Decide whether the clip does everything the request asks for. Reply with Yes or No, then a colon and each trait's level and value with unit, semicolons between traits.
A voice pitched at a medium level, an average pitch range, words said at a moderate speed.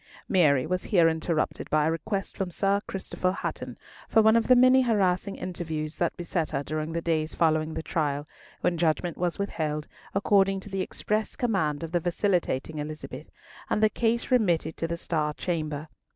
Yes: medium, 170 Hz; average, 4.1 semitones; average, 180 wpm